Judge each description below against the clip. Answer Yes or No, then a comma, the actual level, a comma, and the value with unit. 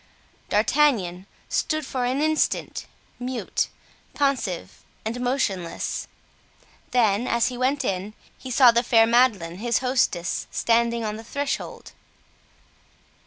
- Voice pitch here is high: Yes, high, 235 Hz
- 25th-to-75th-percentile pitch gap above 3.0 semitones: Yes, average, 3.5 semitones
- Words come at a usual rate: No, slow, 115 wpm